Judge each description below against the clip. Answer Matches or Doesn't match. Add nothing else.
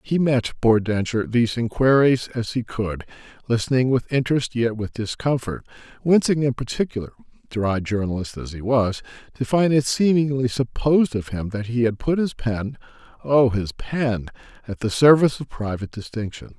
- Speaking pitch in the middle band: Doesn't match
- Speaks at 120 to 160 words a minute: Matches